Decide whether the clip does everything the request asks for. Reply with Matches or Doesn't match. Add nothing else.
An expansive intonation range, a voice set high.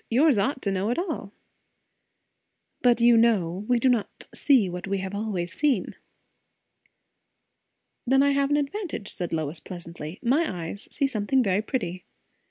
Matches